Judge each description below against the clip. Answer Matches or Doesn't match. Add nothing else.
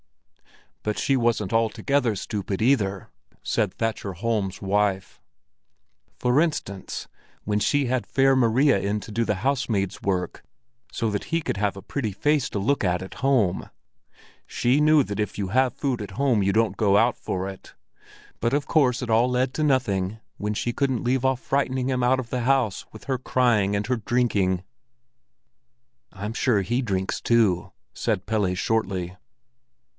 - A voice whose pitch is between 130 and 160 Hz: Doesn't match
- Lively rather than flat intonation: Doesn't match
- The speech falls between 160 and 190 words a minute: Matches